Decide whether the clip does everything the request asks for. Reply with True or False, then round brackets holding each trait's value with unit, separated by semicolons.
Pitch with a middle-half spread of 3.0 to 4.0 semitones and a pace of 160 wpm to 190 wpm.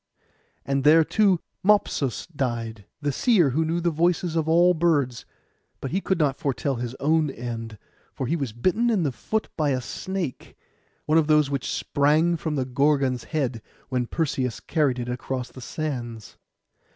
False (4.4 semitones; 170 wpm)